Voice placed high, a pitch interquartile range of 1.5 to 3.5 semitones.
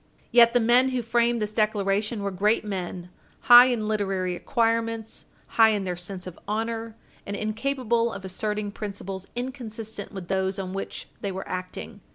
Yes: high, 215 Hz; average, 2.9 semitones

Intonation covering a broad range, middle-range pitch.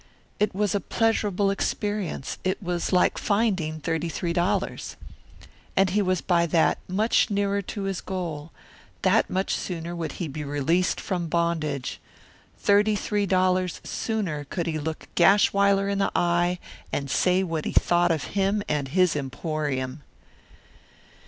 No: average, 3.5 semitones; medium, 180 Hz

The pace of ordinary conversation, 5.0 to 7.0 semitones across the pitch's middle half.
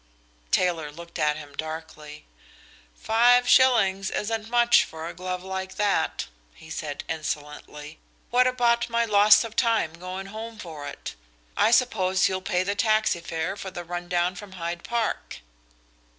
Yes: average, 150 wpm; wide, 5.5 semitones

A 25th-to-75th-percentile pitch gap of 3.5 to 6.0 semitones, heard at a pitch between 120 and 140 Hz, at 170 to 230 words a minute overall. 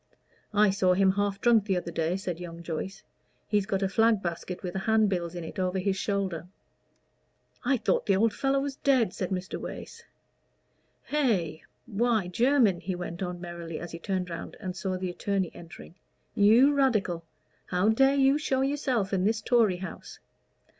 No: average, 4.1 semitones; high, 195 Hz; average, 175 wpm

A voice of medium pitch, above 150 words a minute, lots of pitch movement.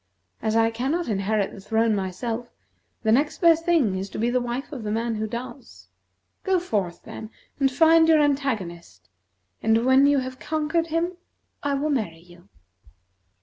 No: high, 240 Hz; average, 170 wpm; wide, 5.7 semitones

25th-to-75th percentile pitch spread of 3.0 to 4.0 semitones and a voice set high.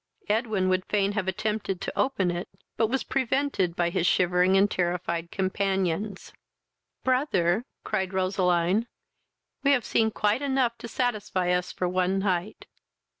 Yes: average, 3.5 semitones; high, 195 Hz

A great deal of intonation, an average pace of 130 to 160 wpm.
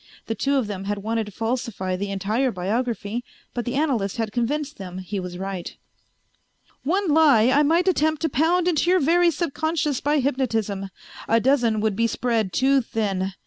No: wide, 6.2 semitones; average, 180 wpm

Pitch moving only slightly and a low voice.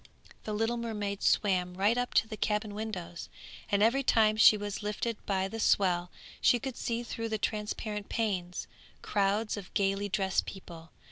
No: narrow, 2.3 semitones; high, 210 Hz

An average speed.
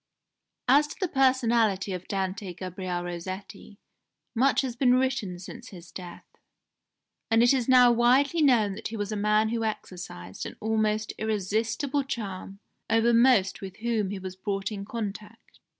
Yes: average, 155 wpm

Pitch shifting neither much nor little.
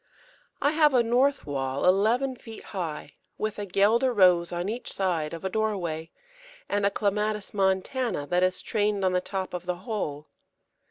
Yes: average, 3.7 semitones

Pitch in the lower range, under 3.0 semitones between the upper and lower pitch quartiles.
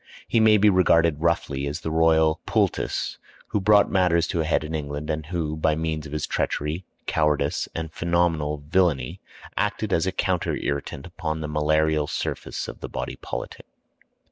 Yes: very low, 80 Hz; narrow, 2.4 semitones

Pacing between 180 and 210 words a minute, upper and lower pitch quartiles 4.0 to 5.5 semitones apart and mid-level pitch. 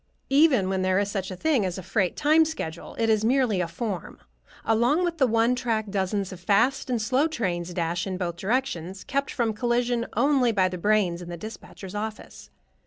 No: average, 195 wpm; average, 4.9 semitones; high, 215 Hz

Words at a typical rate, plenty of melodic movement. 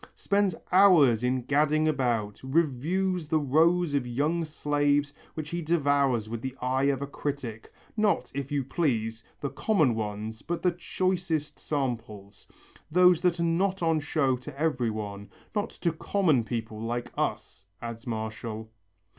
Yes: average, 150 wpm; wide, 5.9 semitones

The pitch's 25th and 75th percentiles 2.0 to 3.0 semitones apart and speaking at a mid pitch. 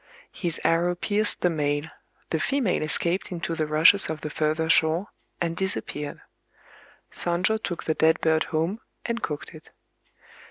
Yes: average, 2.7 semitones; medium, 165 Hz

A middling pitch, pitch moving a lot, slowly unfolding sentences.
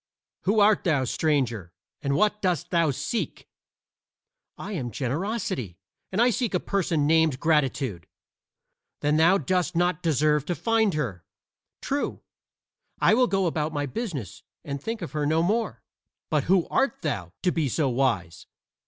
No: medium, 160 Hz; wide, 6.0 semitones; average, 155 wpm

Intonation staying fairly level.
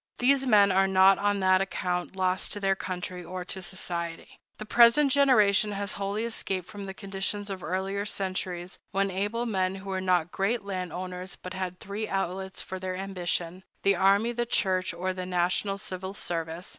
Yes: narrow, 1.7 semitones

